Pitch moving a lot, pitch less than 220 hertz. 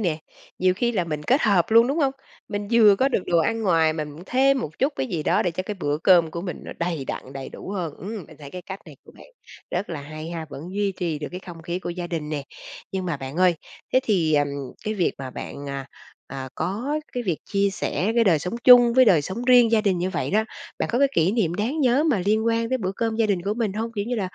Yes: wide, 5.8 semitones; high, 190 Hz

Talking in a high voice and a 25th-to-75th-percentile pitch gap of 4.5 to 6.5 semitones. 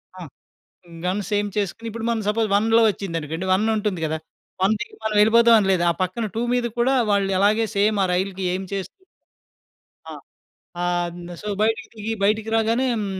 No: high, 210 Hz; average, 2.9 semitones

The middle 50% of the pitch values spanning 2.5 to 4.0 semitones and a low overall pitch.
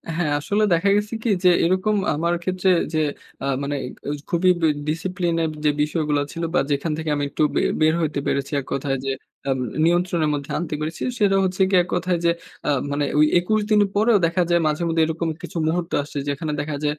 No: average, 3.4 semitones; medium, 165 Hz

